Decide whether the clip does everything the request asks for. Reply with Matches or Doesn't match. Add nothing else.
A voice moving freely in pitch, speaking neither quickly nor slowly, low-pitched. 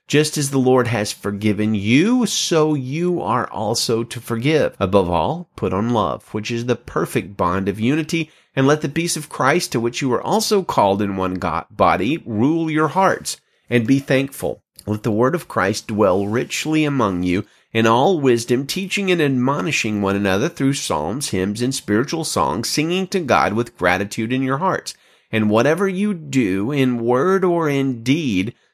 Matches